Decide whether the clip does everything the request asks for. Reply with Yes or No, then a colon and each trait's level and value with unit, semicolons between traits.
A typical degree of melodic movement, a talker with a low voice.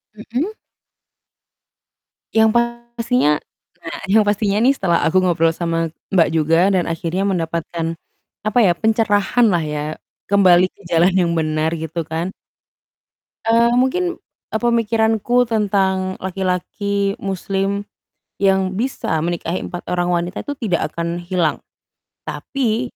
No: average, 4.1 semitones; high, 190 Hz